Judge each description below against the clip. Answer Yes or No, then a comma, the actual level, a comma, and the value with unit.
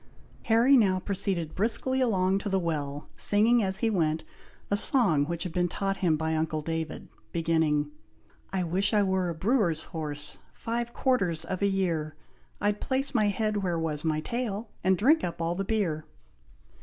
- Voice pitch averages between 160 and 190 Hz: Yes, medium, 185 Hz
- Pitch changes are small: No, average, 4.6 semitones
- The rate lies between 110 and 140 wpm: No, average, 175 wpm